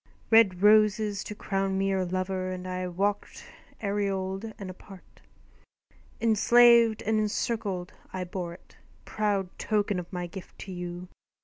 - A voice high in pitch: Yes, high, 195 Hz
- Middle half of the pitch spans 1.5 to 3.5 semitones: Yes, narrow, 2.4 semitones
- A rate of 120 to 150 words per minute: Yes, slow, 135 wpm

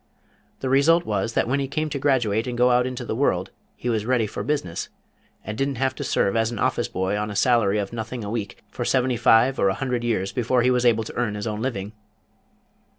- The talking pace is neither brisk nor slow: No, fast, 240 wpm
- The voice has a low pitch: Yes, low, 120 Hz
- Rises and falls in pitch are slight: No, average, 3.4 semitones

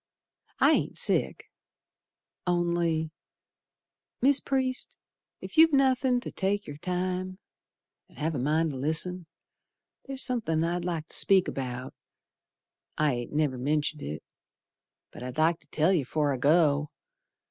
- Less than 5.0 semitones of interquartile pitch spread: Yes, average, 4.0 semitones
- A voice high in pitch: No, medium, 165 Hz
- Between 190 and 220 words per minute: No, slow, 135 wpm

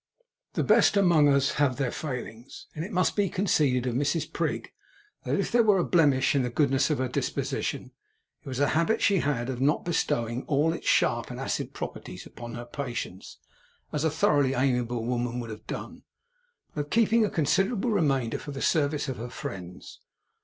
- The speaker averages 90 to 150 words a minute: No, average, 190 wpm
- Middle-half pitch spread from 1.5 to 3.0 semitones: No, average, 4.8 semitones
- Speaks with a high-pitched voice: No, medium, 140 Hz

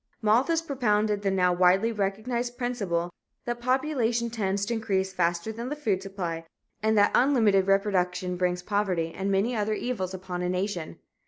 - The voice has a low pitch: No, high, 205 Hz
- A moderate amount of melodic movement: Yes, average, 4.1 semitones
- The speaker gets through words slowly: No, average, 160 wpm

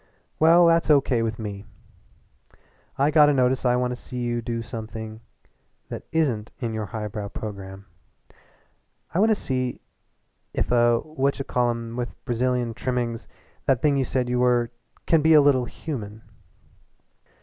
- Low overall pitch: Yes, low, 125 Hz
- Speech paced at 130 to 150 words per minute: No, average, 160 wpm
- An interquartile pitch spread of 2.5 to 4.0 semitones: Yes, average, 3.2 semitones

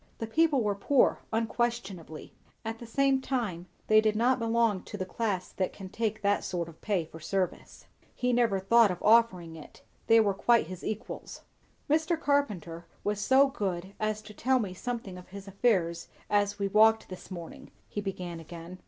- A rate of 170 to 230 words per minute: Yes, average, 180 wpm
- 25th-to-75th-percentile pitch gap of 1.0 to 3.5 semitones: No, average, 4.1 semitones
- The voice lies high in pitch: Yes, high, 210 Hz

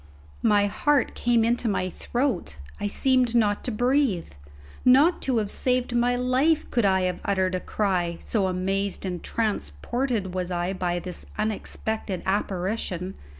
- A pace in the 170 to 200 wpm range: No, average, 150 wpm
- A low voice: No, high, 205 Hz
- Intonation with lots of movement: No, average, 4.8 semitones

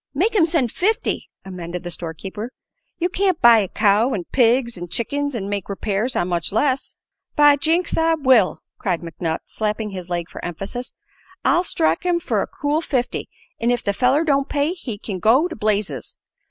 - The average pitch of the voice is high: Yes, high, 235 Hz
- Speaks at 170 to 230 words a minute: Yes, average, 190 wpm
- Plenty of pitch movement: Yes, wide, 7.2 semitones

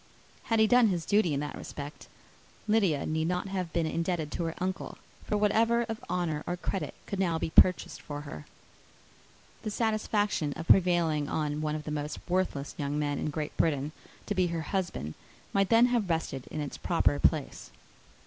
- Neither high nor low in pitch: Yes, medium, 170 Hz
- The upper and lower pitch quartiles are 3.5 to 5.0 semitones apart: Yes, average, 4.6 semitones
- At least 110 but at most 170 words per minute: No, average, 185 wpm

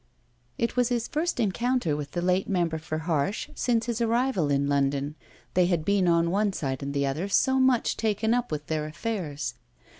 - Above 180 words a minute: Yes, average, 190 wpm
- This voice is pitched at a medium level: Yes, medium, 180 Hz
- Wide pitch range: Yes, wide, 7.3 semitones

